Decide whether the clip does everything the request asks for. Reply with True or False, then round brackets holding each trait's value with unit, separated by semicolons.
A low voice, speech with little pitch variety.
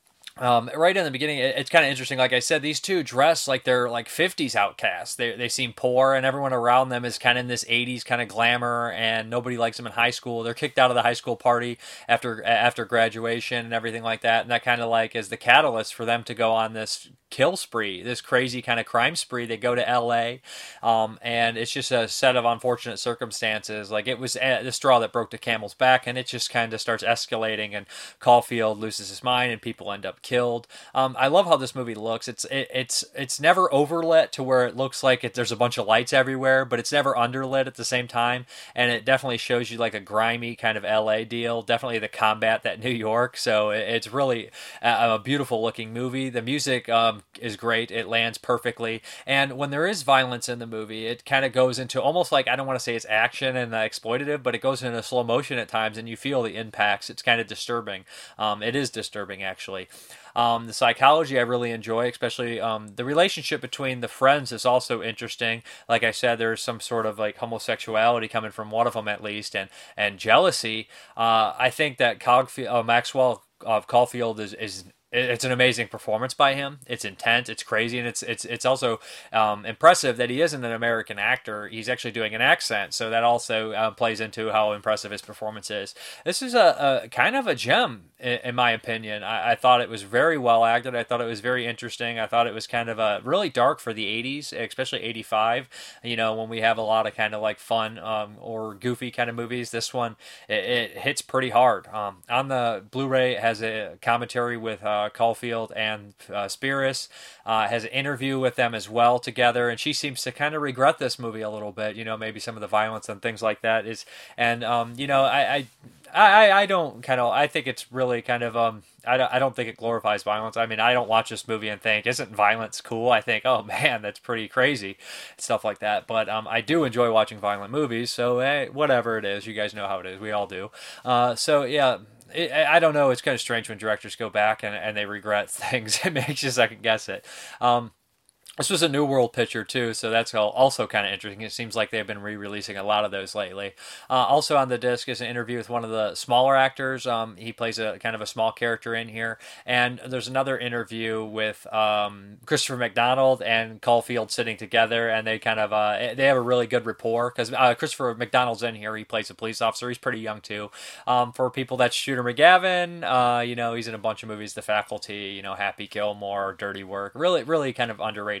True (120 Hz; 2.3 semitones)